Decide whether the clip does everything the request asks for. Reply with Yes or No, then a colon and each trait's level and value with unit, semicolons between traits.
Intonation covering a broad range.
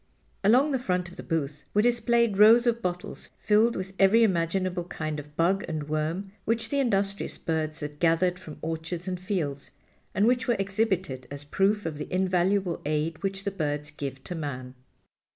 No: average, 4.8 semitones